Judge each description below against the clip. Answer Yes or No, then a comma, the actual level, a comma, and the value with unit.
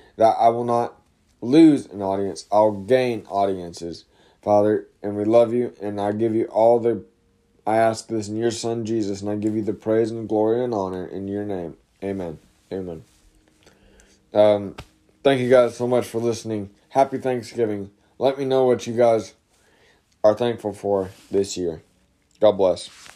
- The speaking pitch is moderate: No, low, 105 Hz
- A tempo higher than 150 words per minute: Yes, average, 170 wpm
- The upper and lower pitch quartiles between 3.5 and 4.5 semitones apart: No, average, 3.1 semitones